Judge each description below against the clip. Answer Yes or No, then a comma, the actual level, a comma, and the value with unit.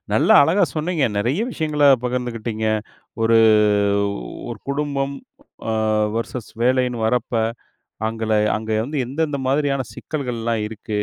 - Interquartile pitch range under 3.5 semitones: No, average, 4.2 semitones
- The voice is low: Yes, low, 125 Hz